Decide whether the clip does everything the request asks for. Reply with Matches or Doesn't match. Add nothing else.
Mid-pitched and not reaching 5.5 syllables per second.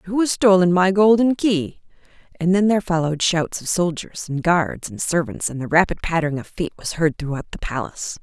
Doesn't match